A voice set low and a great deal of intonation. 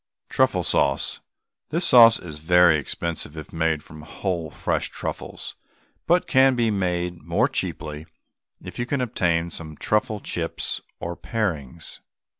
Yes: very low, 85 Hz; wide, 5.9 semitones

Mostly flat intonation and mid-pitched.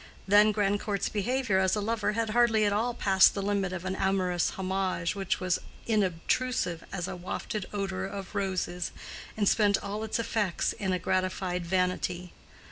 No: narrow, 2.3 semitones; high, 195 Hz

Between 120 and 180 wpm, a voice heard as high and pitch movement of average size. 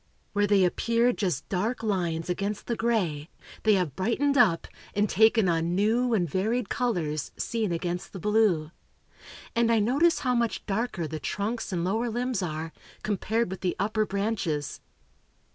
Yes: average, 160 wpm; high, 205 Hz; average, 4.7 semitones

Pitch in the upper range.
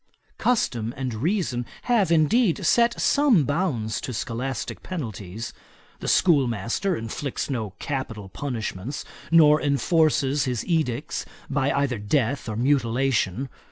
No: low, 135 Hz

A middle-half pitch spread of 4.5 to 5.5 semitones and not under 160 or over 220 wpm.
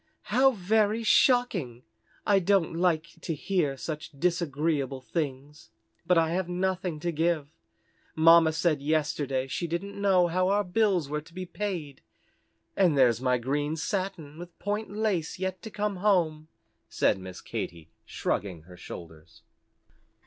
No: average, 4.8 semitones; average, 140 wpm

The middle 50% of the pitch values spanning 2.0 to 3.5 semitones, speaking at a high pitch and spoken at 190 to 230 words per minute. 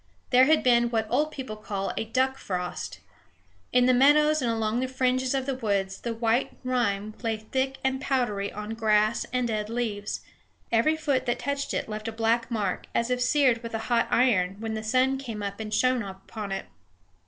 Yes: average, 3.2 semitones; high, 235 Hz; average, 200 wpm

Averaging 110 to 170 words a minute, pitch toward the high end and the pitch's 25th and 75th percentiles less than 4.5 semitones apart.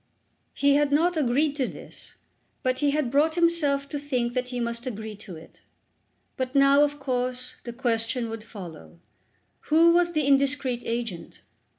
Yes: average, 165 wpm; very high, 260 Hz; average, 3.5 semitones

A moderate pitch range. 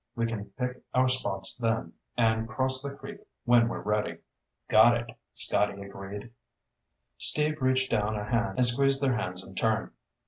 Yes: average, 3.4 semitones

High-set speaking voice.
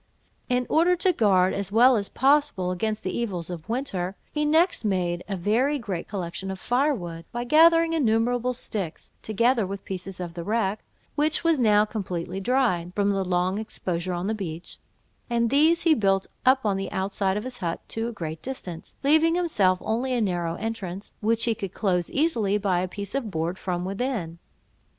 Yes: high, 205 Hz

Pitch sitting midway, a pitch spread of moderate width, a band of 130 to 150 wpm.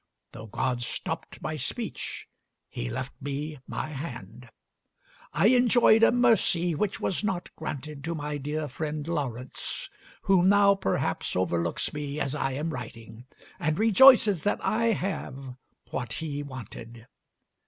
No: medium, 150 Hz; wide, 7.0 semitones; slow, 135 wpm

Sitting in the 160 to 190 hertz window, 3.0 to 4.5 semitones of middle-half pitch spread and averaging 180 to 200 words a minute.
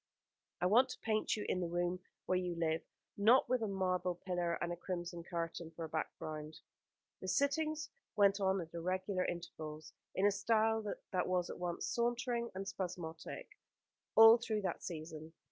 No: medium, 185 Hz; average, 4.1 semitones; average, 170 wpm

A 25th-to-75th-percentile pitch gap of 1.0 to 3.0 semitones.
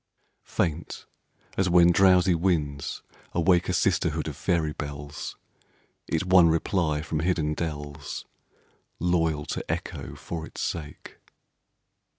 Yes: average, 2.7 semitones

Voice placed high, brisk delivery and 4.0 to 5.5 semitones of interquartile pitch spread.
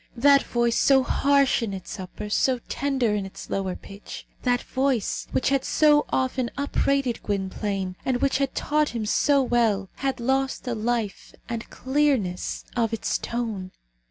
No: high, 240 Hz; average, 155 wpm; average, 4.6 semitones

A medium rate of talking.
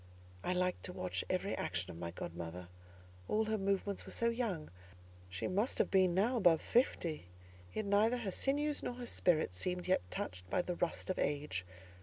Yes: average, 185 wpm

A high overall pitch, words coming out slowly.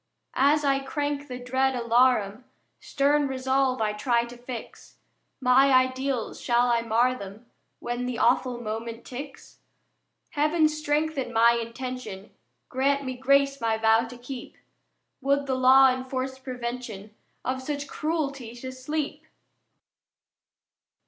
Yes: very high, 255 Hz; slow, 125 wpm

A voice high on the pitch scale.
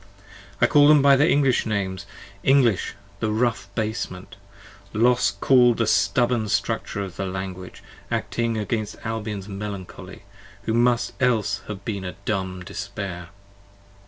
No: low, 110 Hz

